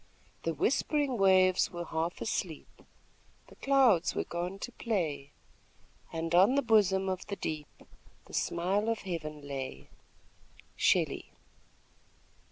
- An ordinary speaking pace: No, slow, 120 wpm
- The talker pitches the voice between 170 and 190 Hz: Yes, medium, 185 Hz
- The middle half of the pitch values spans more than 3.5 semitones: Yes, average, 4.6 semitones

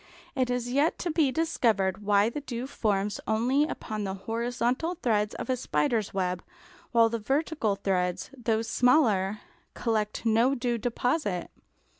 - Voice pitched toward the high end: Yes, high, 230 Hz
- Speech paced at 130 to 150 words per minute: Yes, average, 145 wpm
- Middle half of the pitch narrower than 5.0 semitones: Yes, average, 3.7 semitones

